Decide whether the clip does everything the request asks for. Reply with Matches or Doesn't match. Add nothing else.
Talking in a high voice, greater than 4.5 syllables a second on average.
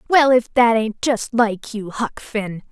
Doesn't match